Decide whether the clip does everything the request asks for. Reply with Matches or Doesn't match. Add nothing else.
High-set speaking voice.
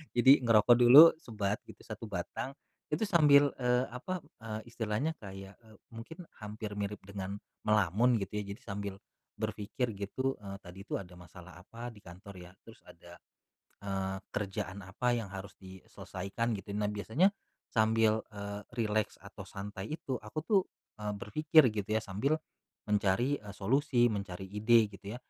Doesn't match